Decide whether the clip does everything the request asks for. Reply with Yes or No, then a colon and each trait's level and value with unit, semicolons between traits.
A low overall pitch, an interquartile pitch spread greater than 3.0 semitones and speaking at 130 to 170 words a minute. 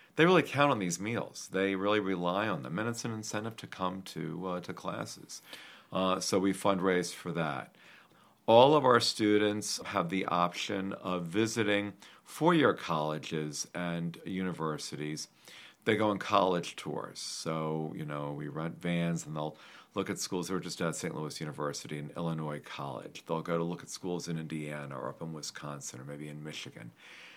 No: very low, 85 Hz; average, 4.1 semitones; average, 180 wpm